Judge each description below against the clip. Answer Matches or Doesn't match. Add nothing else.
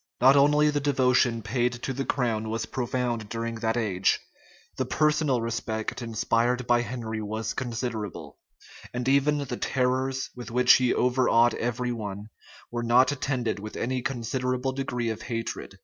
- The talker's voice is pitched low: Matches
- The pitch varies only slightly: Matches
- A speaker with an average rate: Matches